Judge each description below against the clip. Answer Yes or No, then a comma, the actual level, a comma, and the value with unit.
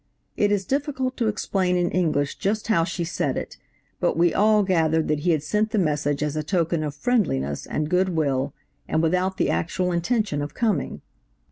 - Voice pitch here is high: No, medium, 175 Hz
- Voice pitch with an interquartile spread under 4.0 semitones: No, average, 5.3 semitones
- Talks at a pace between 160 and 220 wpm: Yes, average, 195 wpm